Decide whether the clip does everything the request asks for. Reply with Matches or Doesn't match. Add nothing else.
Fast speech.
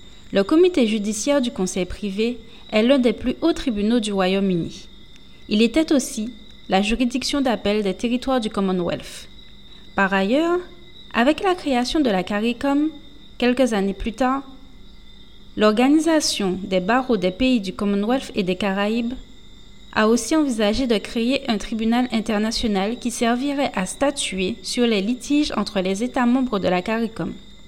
Doesn't match